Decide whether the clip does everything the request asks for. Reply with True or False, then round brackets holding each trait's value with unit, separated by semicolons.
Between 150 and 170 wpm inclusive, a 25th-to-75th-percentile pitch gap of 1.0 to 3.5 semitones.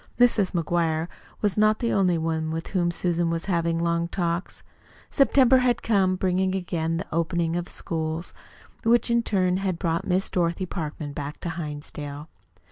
True (165 wpm; 2.7 semitones)